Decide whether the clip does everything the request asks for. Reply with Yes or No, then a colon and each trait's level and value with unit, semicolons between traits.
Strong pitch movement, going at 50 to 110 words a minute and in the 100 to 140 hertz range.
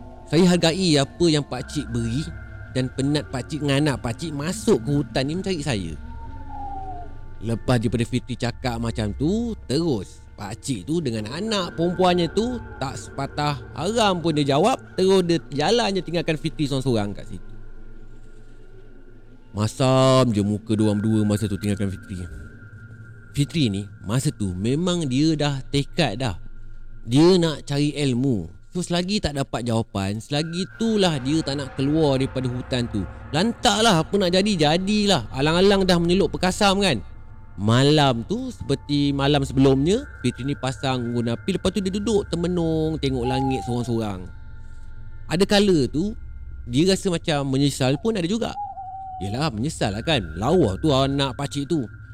No: wide, 7.2 semitones; fast, 155 wpm; low, 135 Hz